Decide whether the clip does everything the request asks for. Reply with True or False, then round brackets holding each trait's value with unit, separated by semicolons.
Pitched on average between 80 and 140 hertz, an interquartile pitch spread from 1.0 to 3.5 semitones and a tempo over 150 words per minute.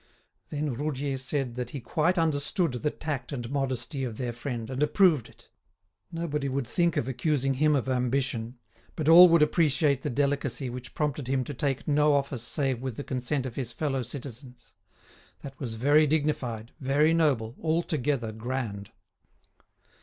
True (135 Hz; 3.1 semitones; 160 wpm)